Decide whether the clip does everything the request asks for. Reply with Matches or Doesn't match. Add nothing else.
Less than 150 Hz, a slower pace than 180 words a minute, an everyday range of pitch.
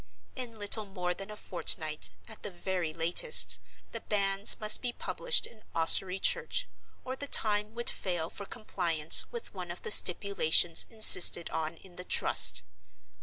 Doesn't match